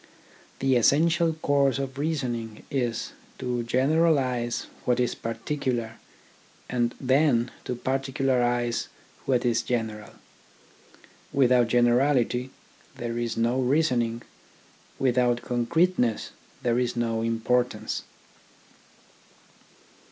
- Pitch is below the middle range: Yes, low, 125 Hz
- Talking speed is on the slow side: Yes, slow, 90 wpm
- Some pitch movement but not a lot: No, narrow, 2.2 semitones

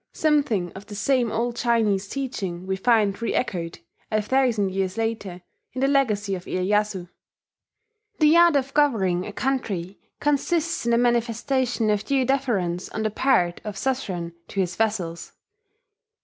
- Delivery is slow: No, average, 150 wpm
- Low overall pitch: No, high, 220 Hz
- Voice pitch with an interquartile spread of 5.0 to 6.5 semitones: Yes, wide, 5.5 semitones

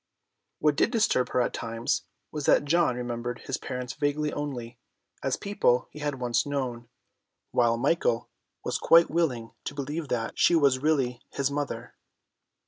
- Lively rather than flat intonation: No, average, 3.5 semitones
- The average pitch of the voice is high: No, low, 135 Hz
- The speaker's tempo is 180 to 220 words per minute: No, average, 155 wpm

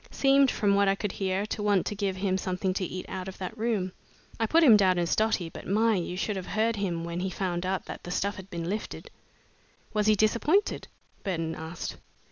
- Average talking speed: No, fast, 225 wpm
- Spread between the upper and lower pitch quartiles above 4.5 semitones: No, average, 2.7 semitones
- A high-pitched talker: Yes, high, 195 Hz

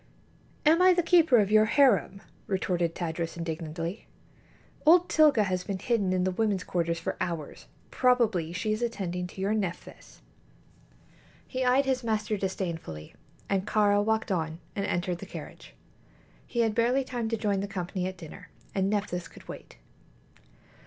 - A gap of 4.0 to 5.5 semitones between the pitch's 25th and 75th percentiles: Yes, average, 4.5 semitones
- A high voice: Yes, high, 200 Hz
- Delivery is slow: No, average, 160 wpm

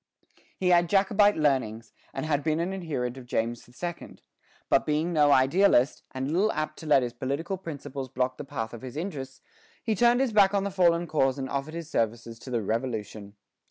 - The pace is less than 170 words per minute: No, average, 195 wpm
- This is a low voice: No, medium, 145 Hz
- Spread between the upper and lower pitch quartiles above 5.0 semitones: Yes, wide, 5.5 semitones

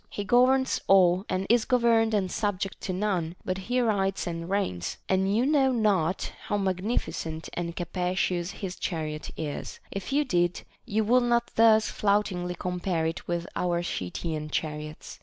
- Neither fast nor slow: Yes, average, 160 wpm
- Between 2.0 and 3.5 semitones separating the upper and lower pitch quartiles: No, average, 3.9 semitones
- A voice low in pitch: No, high, 190 Hz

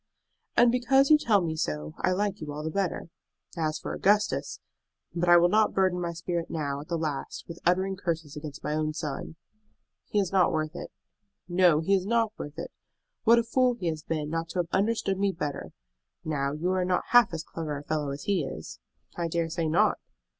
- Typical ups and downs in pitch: Yes, average, 3.9 semitones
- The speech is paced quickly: Yes, fast, 210 wpm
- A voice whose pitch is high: No, medium, 170 Hz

